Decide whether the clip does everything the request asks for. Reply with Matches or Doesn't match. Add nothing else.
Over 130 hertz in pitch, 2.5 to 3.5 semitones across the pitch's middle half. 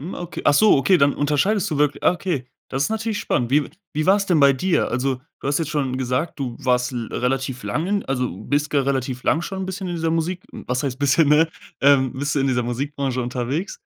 Doesn't match